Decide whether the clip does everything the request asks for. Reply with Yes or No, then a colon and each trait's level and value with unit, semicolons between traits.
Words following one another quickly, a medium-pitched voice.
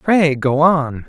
No: average, 165 wpm; medium, 150 Hz